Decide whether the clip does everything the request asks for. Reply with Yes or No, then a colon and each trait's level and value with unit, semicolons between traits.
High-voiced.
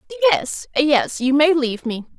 Yes: very high, 285 Hz